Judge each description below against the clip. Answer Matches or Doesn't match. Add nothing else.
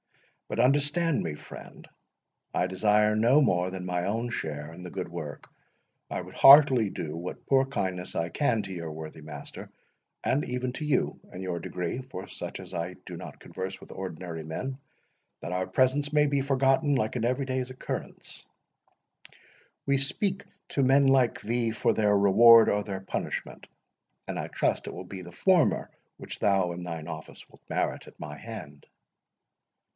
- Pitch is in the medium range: Doesn't match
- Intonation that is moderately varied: Doesn't match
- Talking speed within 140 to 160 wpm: Doesn't match